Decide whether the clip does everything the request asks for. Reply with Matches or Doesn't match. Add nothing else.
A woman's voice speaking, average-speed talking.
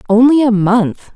Matches